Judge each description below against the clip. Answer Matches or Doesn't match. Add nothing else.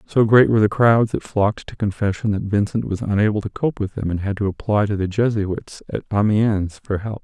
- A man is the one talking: Matches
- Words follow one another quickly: Matches